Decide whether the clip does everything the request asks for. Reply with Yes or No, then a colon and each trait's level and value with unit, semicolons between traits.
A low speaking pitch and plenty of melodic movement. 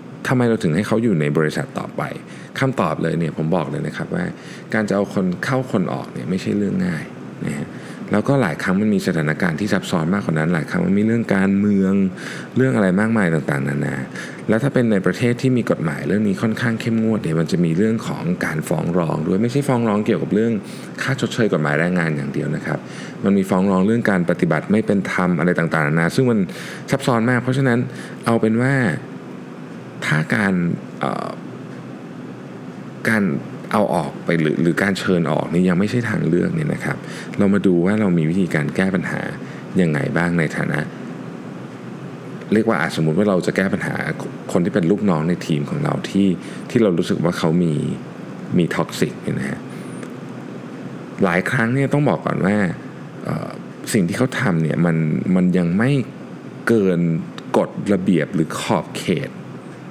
Yes: low, 100 Hz; wide, 5.9 semitones